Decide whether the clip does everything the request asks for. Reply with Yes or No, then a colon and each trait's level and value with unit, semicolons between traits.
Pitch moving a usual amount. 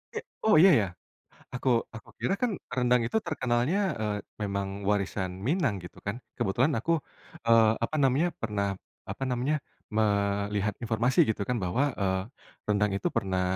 Yes: average, 4.1 semitones